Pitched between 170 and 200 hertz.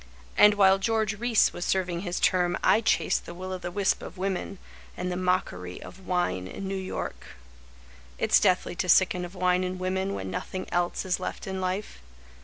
Yes: medium, 185 Hz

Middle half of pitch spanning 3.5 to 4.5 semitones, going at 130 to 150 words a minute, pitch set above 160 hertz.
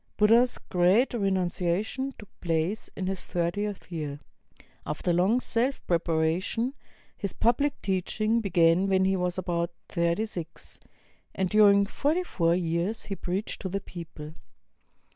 Yes: average, 3.9 semitones; average, 140 wpm; high, 190 Hz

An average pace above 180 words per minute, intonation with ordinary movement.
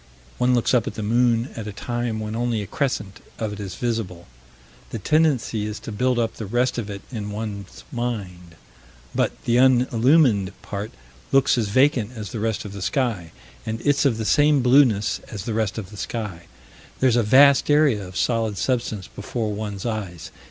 Yes: average, 190 wpm; average, 3.3 semitones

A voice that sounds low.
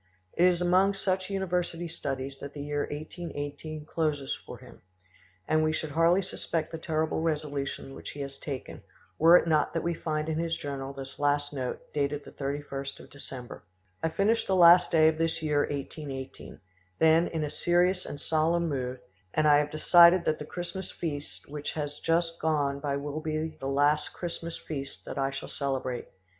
No: medium, 155 Hz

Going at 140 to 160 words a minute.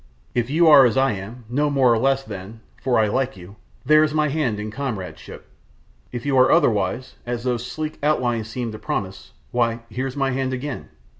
No: average, 195 wpm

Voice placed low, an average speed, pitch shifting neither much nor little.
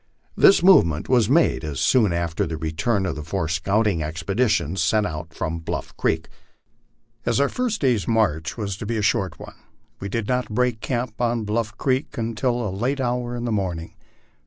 No: low, 105 Hz; average, 180 wpm; wide, 6.4 semitones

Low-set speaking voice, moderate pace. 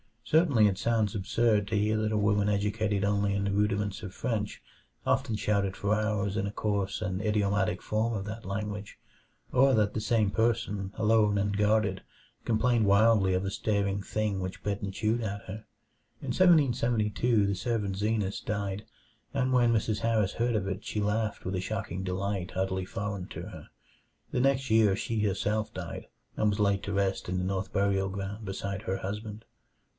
Yes: low, 105 Hz; average, 180 wpm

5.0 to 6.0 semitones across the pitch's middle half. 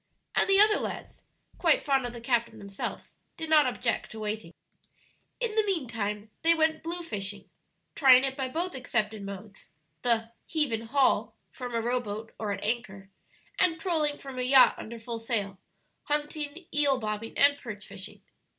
Yes: wide, 5.5 semitones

